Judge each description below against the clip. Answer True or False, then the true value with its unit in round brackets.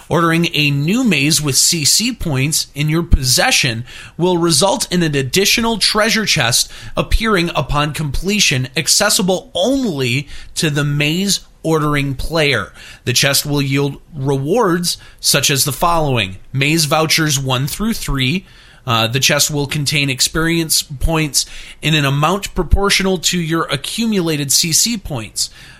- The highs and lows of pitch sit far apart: False (4.2 semitones)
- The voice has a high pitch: False (155 Hz)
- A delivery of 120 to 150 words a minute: True (135 wpm)